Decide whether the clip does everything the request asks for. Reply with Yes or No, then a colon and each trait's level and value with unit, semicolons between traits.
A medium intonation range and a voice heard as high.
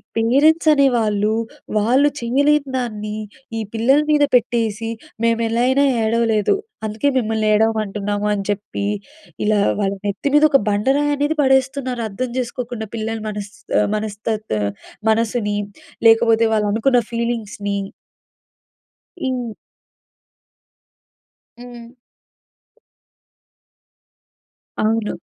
Yes: average, 3.3 semitones; high, 230 Hz